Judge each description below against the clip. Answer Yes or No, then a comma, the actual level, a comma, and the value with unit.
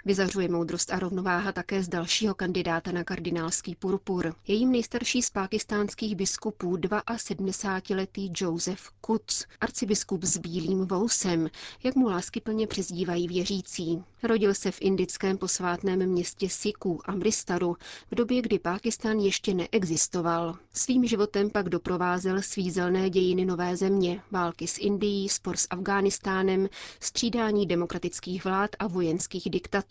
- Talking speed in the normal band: Yes, average, 125 wpm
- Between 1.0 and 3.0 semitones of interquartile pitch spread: Yes, narrow, 2.5 semitones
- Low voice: No, high, 190 Hz